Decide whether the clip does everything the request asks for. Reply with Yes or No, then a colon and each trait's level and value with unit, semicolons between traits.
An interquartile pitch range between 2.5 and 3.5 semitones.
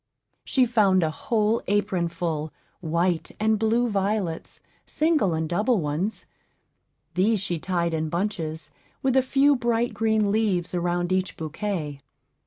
No: average, 4.6 semitones